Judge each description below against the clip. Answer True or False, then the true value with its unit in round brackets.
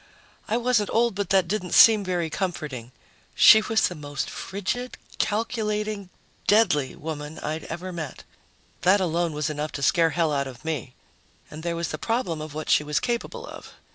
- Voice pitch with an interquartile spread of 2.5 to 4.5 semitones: False (5.6 semitones)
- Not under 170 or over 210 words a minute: True (175 wpm)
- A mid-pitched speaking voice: True (175 Hz)